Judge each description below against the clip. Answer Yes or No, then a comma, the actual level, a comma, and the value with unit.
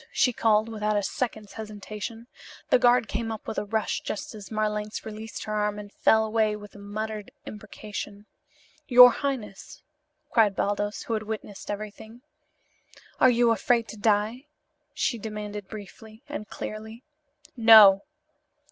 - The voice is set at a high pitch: Yes, high, 215 Hz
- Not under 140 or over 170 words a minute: Yes, average, 145 wpm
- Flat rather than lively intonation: Yes, narrow, 1.5 semitones